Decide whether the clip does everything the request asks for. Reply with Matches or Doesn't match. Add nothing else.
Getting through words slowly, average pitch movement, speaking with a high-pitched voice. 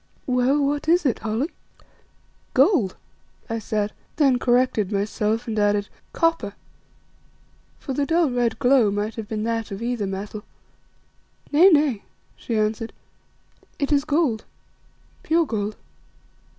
Matches